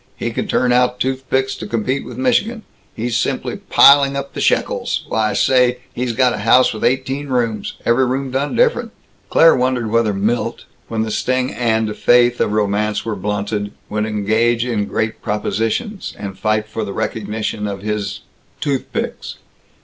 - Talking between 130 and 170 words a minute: Yes, average, 165 wpm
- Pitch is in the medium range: No, low, 115 Hz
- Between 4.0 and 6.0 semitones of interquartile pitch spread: No, average, 3.3 semitones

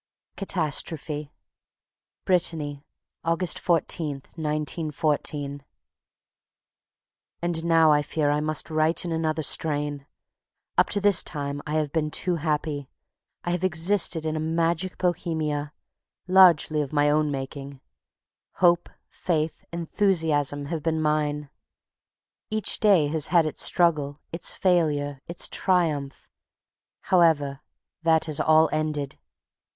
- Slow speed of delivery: Yes, slow, 115 wpm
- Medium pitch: Yes, medium, 155 Hz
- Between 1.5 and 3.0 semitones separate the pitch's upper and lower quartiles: Yes, narrow, 2.4 semitones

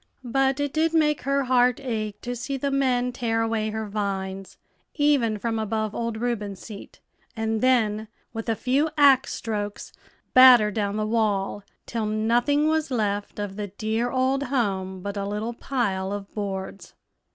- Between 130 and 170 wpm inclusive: Yes, average, 165 wpm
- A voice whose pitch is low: No, high, 225 Hz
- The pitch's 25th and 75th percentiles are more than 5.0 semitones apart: No, average, 3.8 semitones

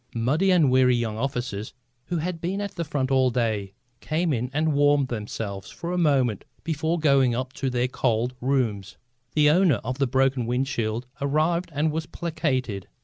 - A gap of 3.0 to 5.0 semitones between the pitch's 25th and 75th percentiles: Yes, average, 4.6 semitones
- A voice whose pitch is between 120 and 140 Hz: Yes, low, 135 Hz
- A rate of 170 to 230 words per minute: Yes, average, 180 wpm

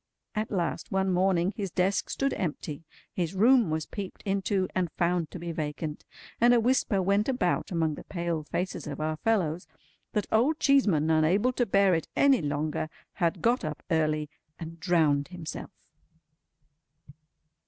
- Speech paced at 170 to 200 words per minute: No, average, 155 wpm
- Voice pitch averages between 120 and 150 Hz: No, medium, 180 Hz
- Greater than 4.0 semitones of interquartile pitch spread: Yes, average, 4.5 semitones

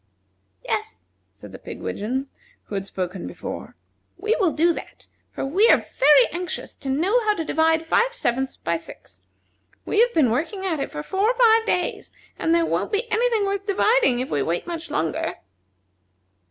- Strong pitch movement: Yes, wide, 8.4 semitones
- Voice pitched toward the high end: Yes, very high, 330 Hz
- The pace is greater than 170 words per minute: Yes, average, 180 wpm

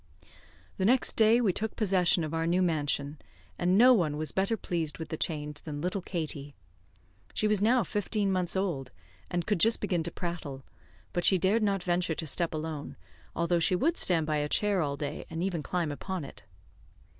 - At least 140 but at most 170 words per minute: No, average, 195 wpm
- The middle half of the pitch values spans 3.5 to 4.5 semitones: Yes, average, 4.0 semitones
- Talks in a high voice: No, medium, 175 Hz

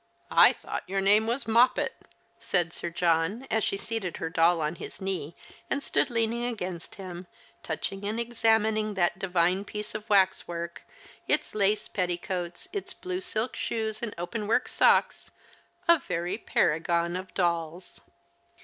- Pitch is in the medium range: No, high, 195 Hz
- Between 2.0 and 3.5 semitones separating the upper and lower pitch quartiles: No, average, 4.2 semitones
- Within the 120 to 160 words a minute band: Yes, average, 155 wpm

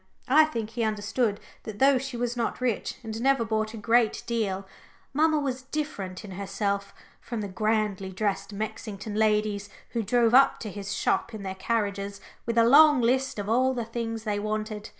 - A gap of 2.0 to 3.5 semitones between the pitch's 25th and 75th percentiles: Yes, average, 2.9 semitones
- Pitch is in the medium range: No, high, 220 Hz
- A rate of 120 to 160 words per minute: No, average, 185 wpm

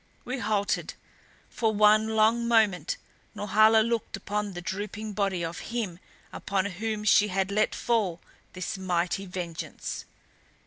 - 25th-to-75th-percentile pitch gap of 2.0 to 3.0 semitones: Yes, narrow, 2.6 semitones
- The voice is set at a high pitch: Yes, high, 205 Hz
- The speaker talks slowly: Yes, slow, 130 wpm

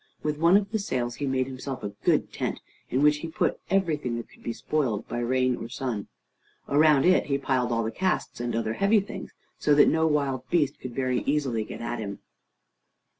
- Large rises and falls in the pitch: No, average, 4.1 semitones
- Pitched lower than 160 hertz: Yes, low, 135 Hz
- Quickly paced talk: Yes, fast, 210 wpm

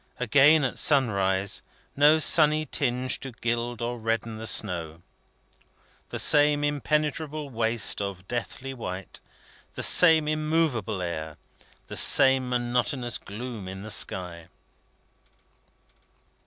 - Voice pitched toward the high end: No, low, 120 Hz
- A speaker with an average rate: No, slow, 110 wpm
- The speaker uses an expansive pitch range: Yes, wide, 6.3 semitones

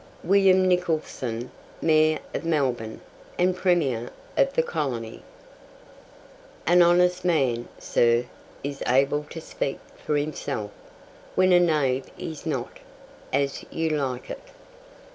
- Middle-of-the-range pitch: Yes, medium, 150 Hz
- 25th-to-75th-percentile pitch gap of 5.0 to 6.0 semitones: Yes, wide, 5.4 semitones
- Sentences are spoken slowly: Yes, slow, 115 wpm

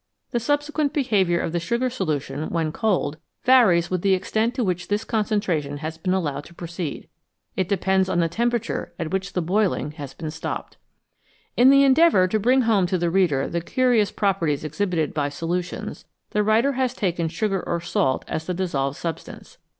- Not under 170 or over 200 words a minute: Yes, average, 180 wpm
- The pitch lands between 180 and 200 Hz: Yes, medium, 185 Hz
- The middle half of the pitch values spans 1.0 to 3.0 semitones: No, average, 5.0 semitones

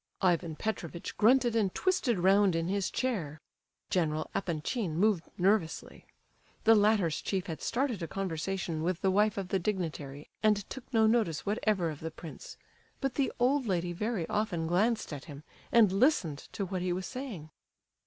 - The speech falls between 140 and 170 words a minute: Yes, average, 165 wpm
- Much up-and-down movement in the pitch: No, average, 4.7 semitones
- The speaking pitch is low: No, high, 190 Hz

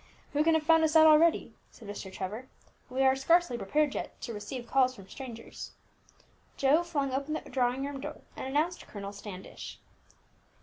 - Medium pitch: No, very high, 270 Hz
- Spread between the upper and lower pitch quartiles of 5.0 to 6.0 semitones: No, average, 4.5 semitones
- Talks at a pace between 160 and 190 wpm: Yes, average, 175 wpm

